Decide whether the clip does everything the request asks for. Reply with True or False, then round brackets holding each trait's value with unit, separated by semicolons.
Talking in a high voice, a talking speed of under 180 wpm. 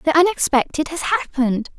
True (285 Hz; 135 wpm)